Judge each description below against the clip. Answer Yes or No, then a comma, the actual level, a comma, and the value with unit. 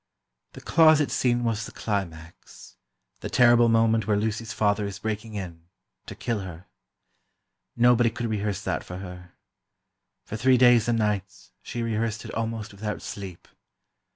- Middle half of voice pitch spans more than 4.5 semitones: No, average, 2.7 semitones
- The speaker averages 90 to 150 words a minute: Yes, average, 145 wpm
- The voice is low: Yes, low, 110 Hz